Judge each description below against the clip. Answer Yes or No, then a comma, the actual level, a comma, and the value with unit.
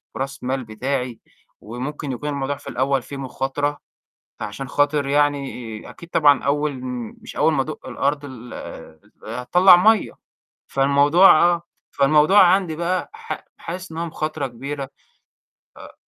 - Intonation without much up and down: No, average, 3.1 semitones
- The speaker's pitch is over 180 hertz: No, medium, 140 Hz